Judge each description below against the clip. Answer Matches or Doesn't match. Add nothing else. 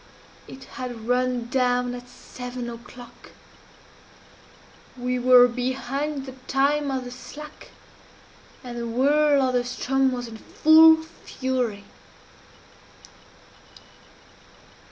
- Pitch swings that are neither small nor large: Doesn't match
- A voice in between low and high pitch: Doesn't match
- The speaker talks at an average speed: Doesn't match